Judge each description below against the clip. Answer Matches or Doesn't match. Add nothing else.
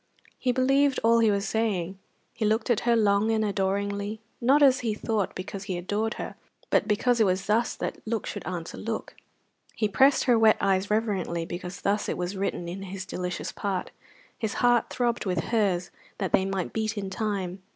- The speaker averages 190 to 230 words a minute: Matches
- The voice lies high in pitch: Matches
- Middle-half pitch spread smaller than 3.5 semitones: Matches